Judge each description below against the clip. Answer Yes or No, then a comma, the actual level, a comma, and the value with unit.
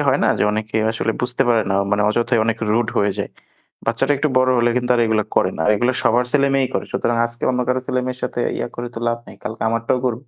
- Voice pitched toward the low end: Yes, low, 120 Hz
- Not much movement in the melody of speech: Yes, narrow, 2.2 semitones